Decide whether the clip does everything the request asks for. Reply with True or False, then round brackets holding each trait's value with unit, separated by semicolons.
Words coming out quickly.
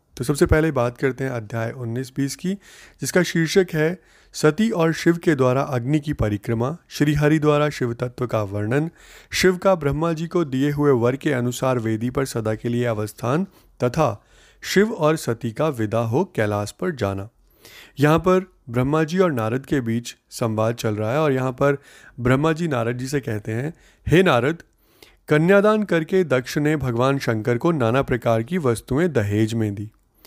False (180 wpm)